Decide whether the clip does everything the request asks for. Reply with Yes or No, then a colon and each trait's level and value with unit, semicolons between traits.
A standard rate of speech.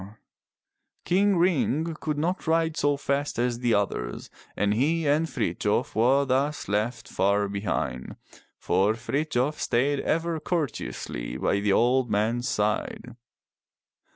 No: slow, 125 wpm